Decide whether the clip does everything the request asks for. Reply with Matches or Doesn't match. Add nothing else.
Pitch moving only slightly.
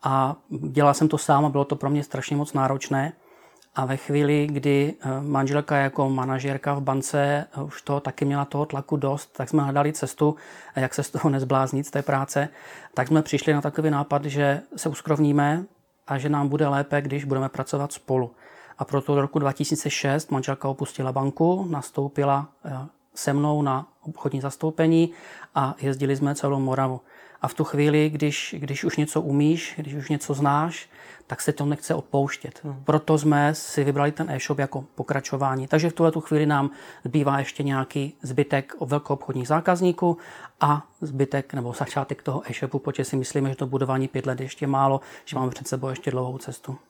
Matches